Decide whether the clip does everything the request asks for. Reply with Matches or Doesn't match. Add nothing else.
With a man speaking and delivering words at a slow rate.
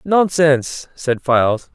Matches